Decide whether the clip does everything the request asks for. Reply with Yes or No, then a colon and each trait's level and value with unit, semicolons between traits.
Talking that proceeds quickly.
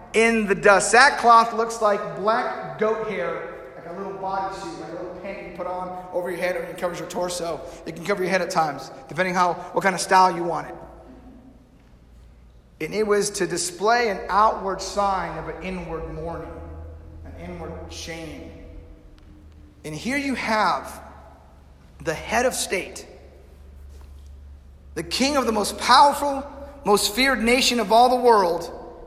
No: average, 165 wpm